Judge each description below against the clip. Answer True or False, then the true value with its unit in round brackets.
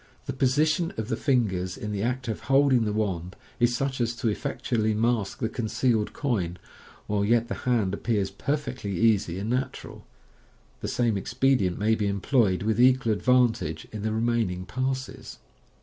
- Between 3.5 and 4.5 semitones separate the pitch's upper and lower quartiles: True (3.8 semitones)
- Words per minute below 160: False (175 wpm)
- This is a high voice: False (115 Hz)